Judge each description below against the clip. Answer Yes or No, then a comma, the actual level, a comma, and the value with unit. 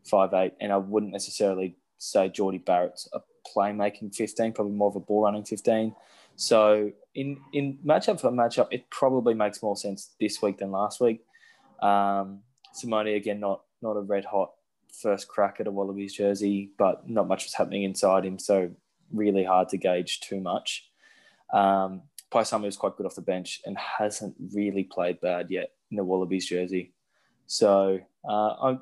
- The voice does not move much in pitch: Yes, narrow, 1.7 semitones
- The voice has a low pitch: Yes, low, 100 Hz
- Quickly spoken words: No, average, 175 wpm